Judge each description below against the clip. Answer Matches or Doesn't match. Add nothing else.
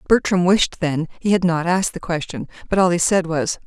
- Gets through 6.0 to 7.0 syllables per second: Doesn't match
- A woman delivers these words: Matches